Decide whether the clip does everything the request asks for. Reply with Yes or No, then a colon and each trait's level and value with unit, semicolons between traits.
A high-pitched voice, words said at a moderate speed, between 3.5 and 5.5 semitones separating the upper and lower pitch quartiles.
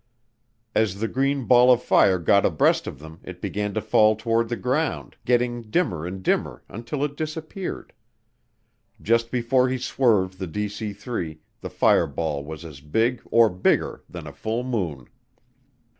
No: low, 110 Hz; average, 160 wpm; average, 5.2 semitones